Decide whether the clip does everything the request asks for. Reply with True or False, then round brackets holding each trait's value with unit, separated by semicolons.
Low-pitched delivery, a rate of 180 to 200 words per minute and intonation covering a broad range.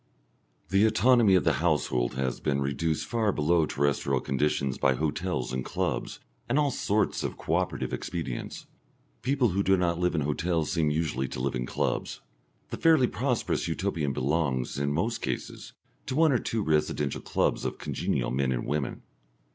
False (80 Hz; 170 wpm; 6.3 semitones)